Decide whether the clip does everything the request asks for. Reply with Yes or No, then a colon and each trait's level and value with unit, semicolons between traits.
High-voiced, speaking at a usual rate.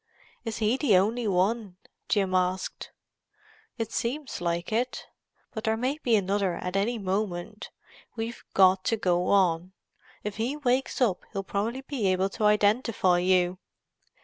Yes: high, 205 Hz; average, 150 wpm